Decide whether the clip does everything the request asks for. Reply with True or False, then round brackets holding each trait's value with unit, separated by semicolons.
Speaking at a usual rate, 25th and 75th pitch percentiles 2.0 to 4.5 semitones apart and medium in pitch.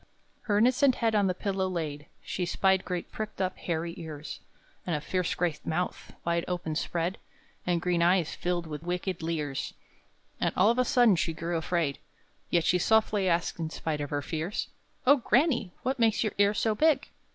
True (185 wpm; 4.1 semitones; 180 Hz)